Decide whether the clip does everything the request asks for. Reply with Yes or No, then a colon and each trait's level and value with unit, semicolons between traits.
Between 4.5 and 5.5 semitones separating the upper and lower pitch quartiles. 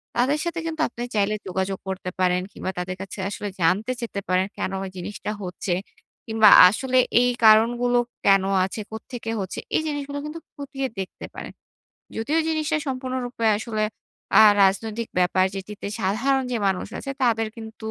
Yes: average, 5.0 semitones